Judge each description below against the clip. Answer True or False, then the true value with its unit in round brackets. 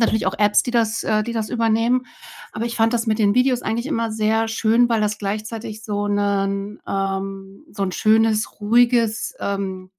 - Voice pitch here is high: True (220 Hz)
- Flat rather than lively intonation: True (2.1 semitones)